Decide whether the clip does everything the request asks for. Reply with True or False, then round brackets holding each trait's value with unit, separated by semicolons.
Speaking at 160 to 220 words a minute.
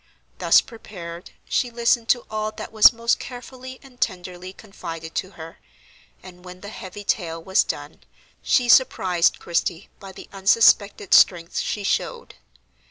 False (145 wpm)